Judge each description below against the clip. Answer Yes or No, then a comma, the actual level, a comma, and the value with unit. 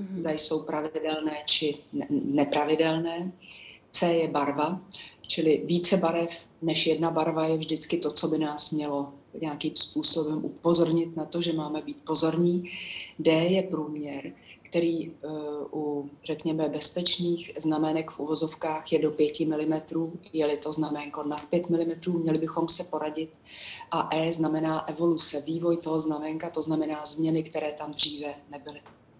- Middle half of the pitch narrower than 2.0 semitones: Yes, narrow, 1.6 semitones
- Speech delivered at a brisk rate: No, average, 140 wpm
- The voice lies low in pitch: No, medium, 155 Hz